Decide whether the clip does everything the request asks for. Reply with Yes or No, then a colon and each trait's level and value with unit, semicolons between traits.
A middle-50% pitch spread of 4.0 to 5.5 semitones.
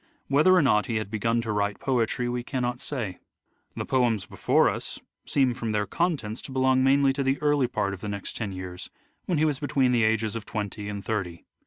Yes: average, 4.3 semitones